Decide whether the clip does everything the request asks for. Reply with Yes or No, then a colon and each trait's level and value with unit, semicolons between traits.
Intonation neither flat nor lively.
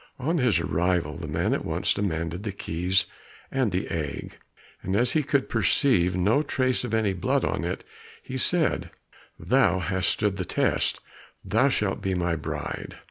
No: wide, 6.0 semitones